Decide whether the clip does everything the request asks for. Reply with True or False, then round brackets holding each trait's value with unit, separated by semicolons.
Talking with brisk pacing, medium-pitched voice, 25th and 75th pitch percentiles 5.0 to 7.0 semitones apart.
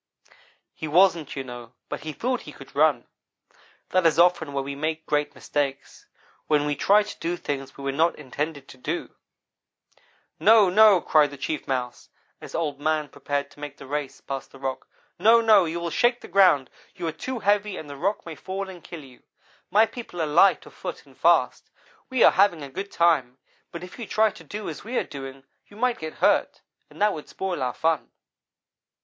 True (210 wpm; 160 Hz; 5.4 semitones)